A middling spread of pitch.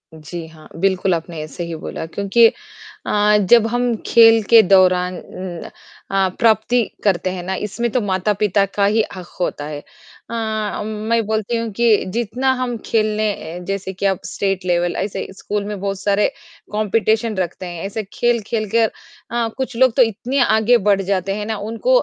Yes: average, 3.4 semitones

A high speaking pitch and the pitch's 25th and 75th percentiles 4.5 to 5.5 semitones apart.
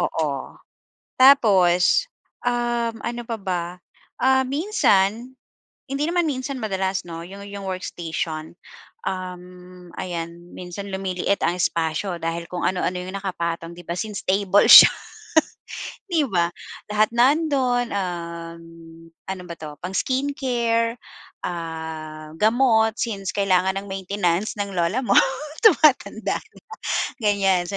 Yes: high, 195 Hz; average, 5.2 semitones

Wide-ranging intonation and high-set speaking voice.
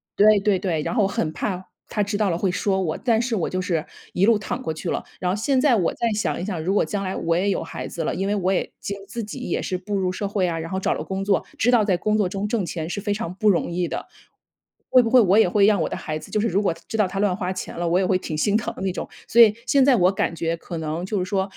No: average, 2.9 semitones; high, 195 Hz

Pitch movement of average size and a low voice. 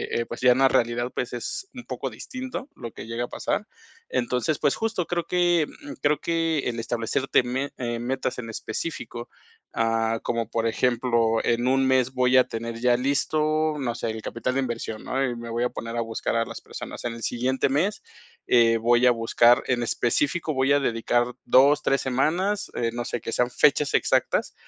Yes: average, 3.3 semitones; low, 125 Hz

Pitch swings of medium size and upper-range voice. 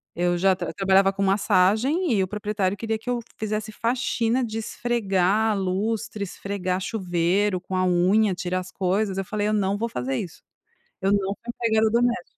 Yes: average, 3.0 semitones; high, 200 Hz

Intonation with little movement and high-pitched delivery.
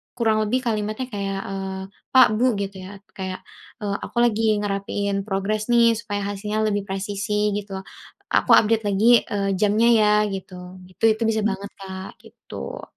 Yes: narrow, 1.8 semitones; high, 205 Hz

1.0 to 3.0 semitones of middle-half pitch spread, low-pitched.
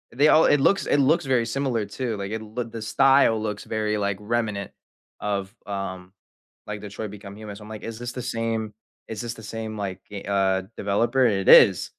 Yes: average, 2.7 semitones; low, 110 Hz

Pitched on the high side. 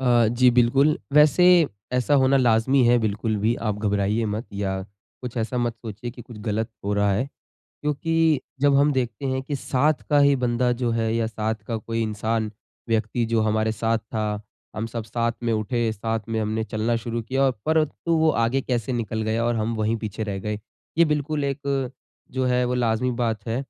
No: low, 115 Hz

